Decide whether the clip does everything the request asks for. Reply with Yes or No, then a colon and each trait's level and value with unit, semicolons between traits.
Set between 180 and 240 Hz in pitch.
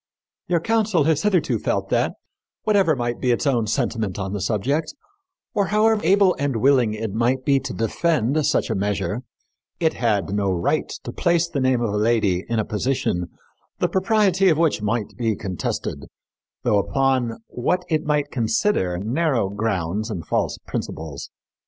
No: low, 120 Hz